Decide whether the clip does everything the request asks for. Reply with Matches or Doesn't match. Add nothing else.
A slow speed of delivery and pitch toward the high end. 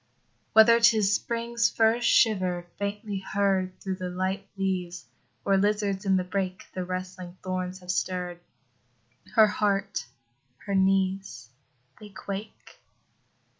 Matches